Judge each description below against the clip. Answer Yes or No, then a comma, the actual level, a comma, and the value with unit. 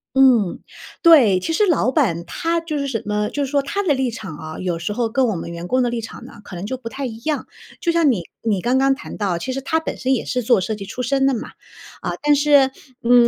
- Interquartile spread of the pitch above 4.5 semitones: Yes, average, 5.1 semitones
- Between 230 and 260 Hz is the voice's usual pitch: Yes, very high, 250 Hz